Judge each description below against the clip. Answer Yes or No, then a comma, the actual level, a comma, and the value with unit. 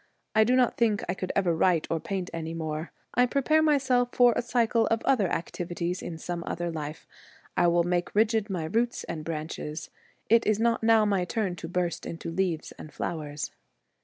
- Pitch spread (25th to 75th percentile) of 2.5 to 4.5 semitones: No, wide, 5.5 semitones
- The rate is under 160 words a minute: No, average, 190 wpm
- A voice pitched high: No, medium, 180 Hz